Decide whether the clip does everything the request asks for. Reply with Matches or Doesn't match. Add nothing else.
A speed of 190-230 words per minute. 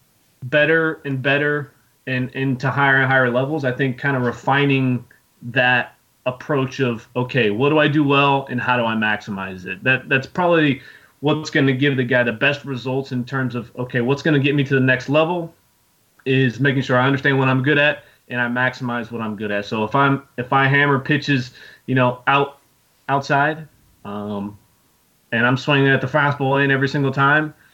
Matches